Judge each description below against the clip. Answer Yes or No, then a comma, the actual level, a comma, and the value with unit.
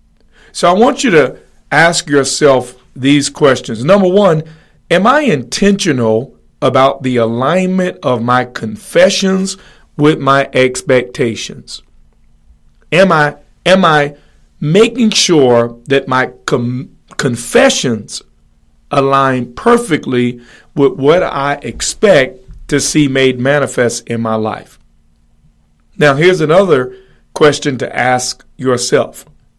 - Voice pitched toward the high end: No, low, 135 Hz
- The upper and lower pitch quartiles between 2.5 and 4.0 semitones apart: No, average, 4.5 semitones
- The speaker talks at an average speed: No, slow, 105 wpm